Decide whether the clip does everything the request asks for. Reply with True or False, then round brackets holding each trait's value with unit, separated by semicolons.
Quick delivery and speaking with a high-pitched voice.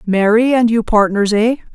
False (135 wpm; 220 Hz)